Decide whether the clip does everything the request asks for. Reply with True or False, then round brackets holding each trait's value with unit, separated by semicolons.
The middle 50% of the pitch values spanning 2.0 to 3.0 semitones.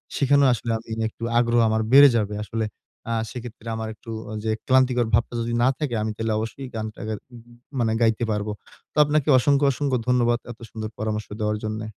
True (2.6 semitones)